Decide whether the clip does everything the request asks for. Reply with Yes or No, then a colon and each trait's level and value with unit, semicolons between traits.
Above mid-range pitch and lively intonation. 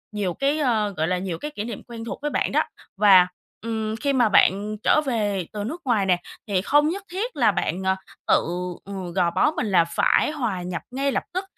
Yes: high, 215 Hz; wide, 6.5 semitones